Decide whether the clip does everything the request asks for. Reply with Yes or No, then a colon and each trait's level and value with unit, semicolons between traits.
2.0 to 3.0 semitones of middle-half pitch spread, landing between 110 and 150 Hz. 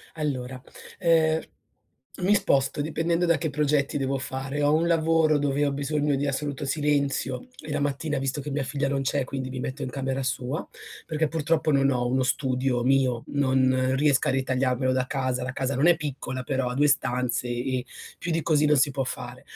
Yes: narrow, 2.4 semitones; medium, 140 Hz